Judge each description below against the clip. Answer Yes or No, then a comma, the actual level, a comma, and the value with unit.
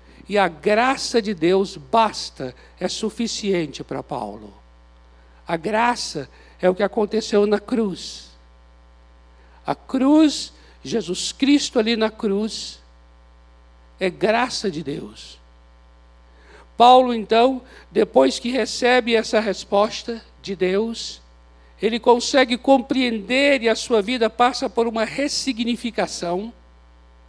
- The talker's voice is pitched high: Yes, high, 205 Hz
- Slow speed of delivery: Yes, slow, 110 wpm